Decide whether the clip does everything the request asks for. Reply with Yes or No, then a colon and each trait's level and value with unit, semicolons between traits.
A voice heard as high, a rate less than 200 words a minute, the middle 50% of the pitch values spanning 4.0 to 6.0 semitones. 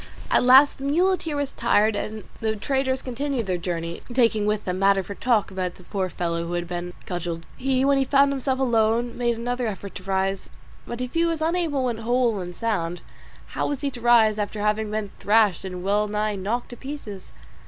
No: high, 220 Hz; fast, 205 wpm; average, 5.0 semitones